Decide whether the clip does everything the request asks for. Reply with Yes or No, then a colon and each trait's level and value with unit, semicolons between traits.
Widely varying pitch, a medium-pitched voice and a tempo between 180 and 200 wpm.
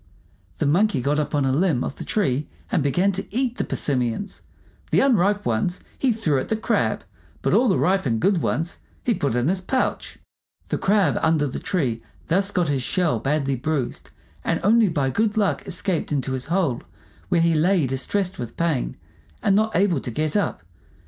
Yes: wide, 6.4 semitones; medium, 165 Hz; average, 195 wpm